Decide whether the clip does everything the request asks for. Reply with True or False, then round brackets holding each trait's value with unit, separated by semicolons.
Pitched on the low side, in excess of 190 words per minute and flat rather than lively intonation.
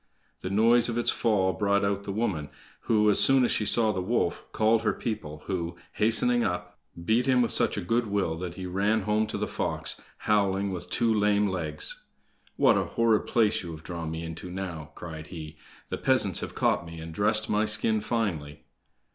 False (100 Hz; 200 wpm; 4.0 semitones)